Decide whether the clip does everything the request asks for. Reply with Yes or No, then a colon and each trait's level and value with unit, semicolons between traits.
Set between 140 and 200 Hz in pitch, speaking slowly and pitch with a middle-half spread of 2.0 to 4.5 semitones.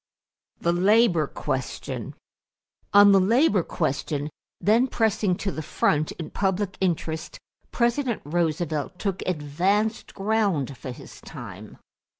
No: medium, 185 Hz; slow, 115 wpm; average, 5.2 semitones